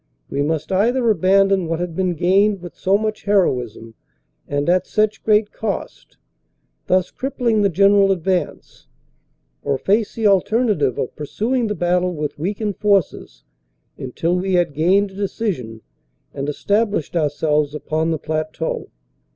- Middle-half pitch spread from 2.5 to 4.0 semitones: No, average, 4.7 semitones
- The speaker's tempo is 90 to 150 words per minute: Yes, average, 140 wpm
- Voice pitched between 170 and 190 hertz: Yes, medium, 185 Hz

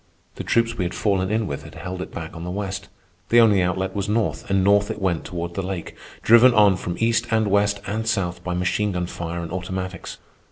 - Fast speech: Yes, fast, 230 wpm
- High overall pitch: No, very low, 95 Hz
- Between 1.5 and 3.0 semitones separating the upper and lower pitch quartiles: Yes, average, 2.7 semitones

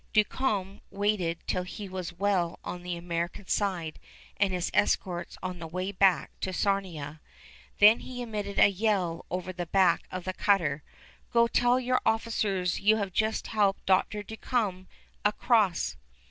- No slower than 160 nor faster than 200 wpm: No, average, 150 wpm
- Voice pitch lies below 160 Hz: No, high, 195 Hz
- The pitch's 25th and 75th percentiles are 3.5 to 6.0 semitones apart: No, average, 2.9 semitones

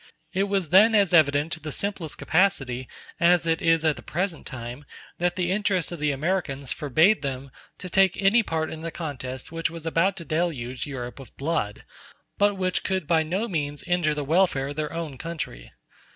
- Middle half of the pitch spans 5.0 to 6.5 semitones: No, average, 4.2 semitones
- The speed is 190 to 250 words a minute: Yes, average, 195 wpm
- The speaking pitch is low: No, medium, 165 Hz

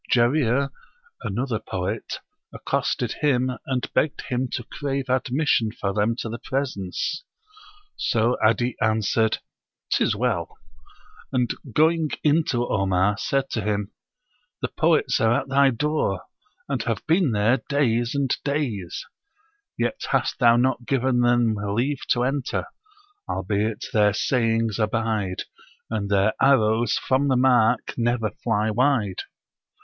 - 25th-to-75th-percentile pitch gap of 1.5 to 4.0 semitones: Yes, average, 3.7 semitones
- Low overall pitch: Yes, low, 120 Hz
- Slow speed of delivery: Yes, slow, 130 wpm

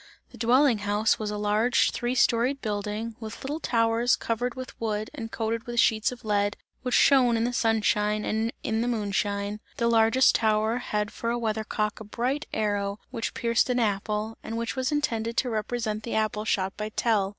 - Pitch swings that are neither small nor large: No, narrow, 2.2 semitones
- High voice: Yes, high, 225 Hz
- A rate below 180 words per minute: No, average, 195 wpm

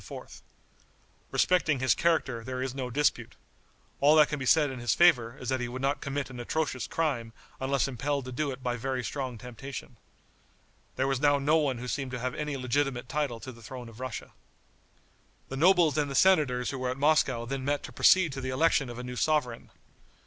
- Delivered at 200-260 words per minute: Yes, fast, 205 wpm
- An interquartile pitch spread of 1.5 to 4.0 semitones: Yes, average, 2.7 semitones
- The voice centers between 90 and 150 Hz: Yes, low, 135 Hz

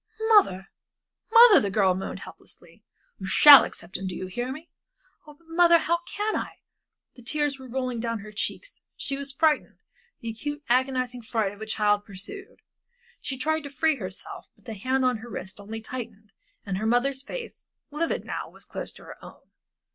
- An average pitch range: No, wide, 5.9 semitones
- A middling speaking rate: Yes, average, 185 wpm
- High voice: Yes, very high, 255 Hz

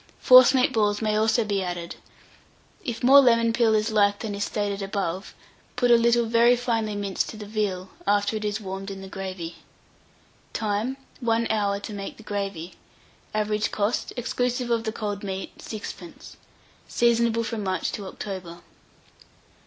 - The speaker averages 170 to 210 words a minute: No, average, 160 wpm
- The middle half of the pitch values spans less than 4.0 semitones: Yes, narrow, 2.6 semitones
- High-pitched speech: Yes, high, 210 Hz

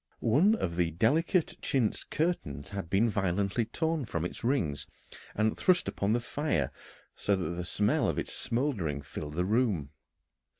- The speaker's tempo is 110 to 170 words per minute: Yes, average, 160 wpm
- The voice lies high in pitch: No, low, 100 Hz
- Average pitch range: No, wide, 7.4 semitones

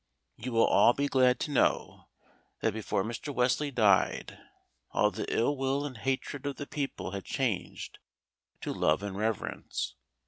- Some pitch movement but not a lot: Yes, average, 4.1 semitones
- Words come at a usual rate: Yes, average, 160 wpm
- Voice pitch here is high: No, low, 125 Hz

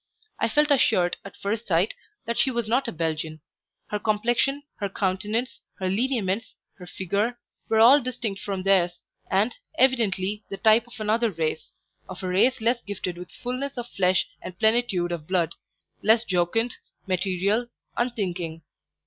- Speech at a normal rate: Yes, average, 155 wpm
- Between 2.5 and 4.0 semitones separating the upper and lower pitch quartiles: No, average, 4.4 semitones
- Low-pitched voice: No, high, 210 Hz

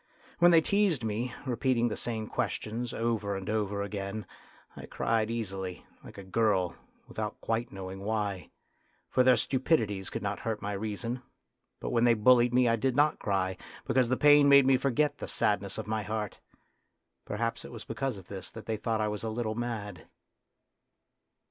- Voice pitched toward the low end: Yes, low, 110 Hz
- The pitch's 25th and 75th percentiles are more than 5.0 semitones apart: No, average, 3.2 semitones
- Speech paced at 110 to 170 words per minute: No, average, 180 wpm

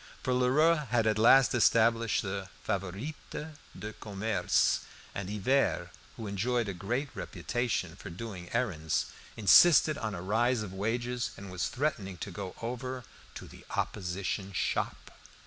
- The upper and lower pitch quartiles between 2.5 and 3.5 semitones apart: No, average, 4.4 semitones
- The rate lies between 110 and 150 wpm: Yes, average, 140 wpm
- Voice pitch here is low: Yes, low, 110 Hz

